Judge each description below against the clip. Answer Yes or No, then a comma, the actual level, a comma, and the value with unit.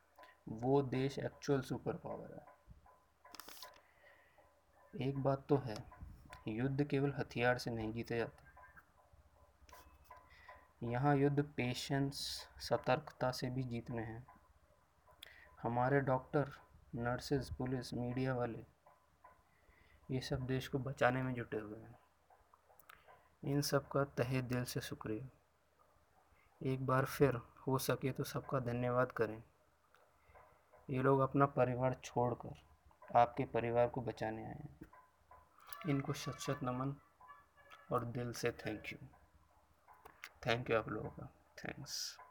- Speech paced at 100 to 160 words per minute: Yes, average, 115 wpm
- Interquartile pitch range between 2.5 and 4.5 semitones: Yes, average, 2.9 semitones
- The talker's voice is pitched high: No, low, 130 Hz